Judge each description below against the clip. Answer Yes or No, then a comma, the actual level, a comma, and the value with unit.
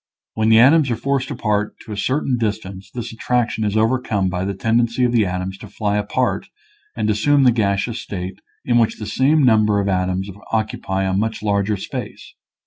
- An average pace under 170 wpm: No, average, 195 wpm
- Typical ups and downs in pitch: Yes, average, 3.2 semitones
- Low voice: Yes, low, 110 Hz